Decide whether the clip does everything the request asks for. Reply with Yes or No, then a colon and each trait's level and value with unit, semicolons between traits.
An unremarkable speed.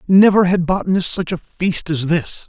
Yes: average, 195 wpm